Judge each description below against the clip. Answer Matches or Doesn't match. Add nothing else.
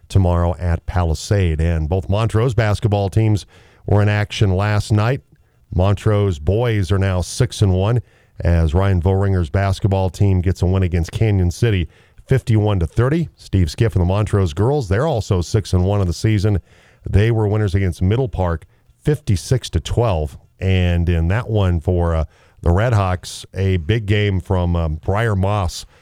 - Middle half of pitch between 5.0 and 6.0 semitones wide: Doesn't match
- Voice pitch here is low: Matches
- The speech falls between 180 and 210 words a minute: Doesn't match